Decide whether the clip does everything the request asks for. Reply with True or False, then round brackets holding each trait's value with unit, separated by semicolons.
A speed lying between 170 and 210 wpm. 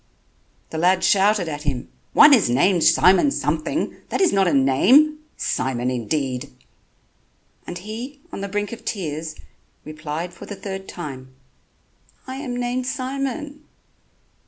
False (135 wpm)